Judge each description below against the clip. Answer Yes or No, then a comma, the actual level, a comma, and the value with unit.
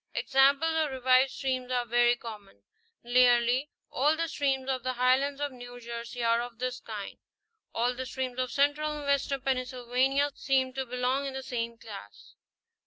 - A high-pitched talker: Yes, very high, 255 Hz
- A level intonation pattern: Yes, narrow, 1.9 semitones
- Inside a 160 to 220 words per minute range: Yes, average, 170 wpm